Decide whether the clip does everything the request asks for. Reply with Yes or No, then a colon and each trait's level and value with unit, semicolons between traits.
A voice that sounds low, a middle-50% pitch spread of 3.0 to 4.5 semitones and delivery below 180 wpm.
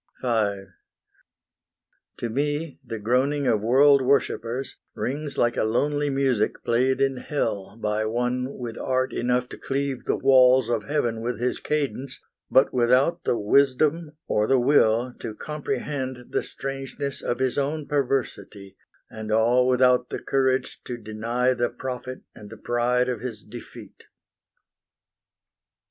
No: low, 125 Hz; narrow, 2.6 semitones; average, 140 wpm